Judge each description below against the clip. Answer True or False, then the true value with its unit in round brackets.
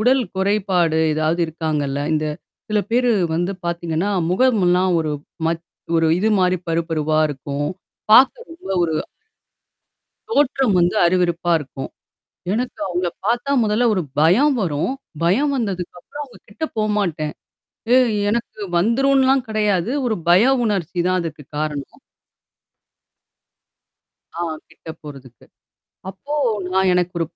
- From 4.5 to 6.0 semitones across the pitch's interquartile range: True (5.2 semitones)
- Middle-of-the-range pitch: True (180 Hz)